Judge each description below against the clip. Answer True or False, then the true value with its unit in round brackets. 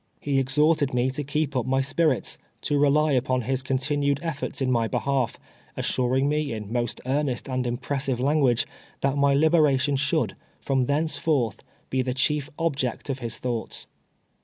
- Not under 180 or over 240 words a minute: False (170 wpm)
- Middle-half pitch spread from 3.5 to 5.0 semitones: False (2.4 semitones)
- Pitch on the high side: False (135 Hz)